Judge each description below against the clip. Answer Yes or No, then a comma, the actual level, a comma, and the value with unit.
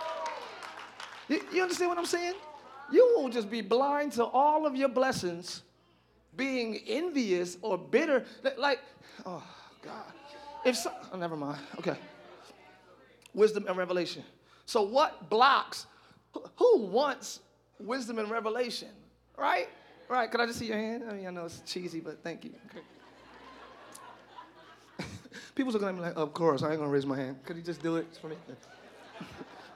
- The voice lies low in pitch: No, high, 235 Hz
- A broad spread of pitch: Yes, wide, 8.0 semitones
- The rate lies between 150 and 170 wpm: Yes, average, 160 wpm